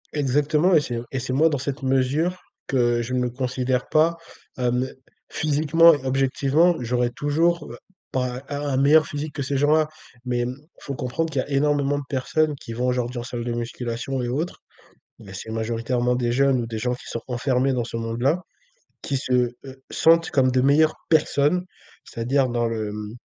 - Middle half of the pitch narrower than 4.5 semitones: Yes, average, 3.2 semitones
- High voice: No, low, 130 Hz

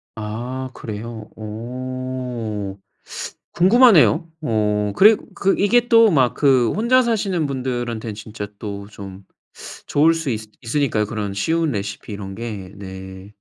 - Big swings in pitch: Yes, wide, 6.5 semitones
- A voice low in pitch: Yes, low, 115 Hz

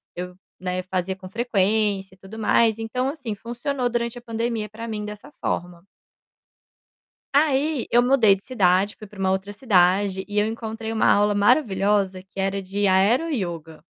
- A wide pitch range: No, average, 3.4 semitones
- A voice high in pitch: Yes, high, 210 Hz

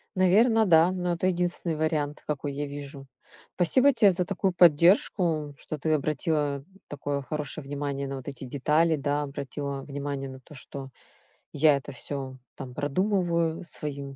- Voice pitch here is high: No, medium, 150 Hz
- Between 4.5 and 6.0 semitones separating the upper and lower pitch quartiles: No, average, 3.5 semitones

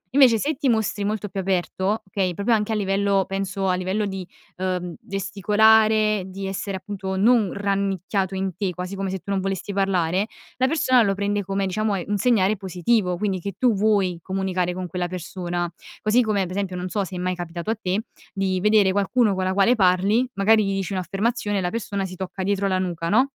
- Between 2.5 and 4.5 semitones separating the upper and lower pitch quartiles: No, narrow, 2.1 semitones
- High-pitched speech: Yes, high, 195 Hz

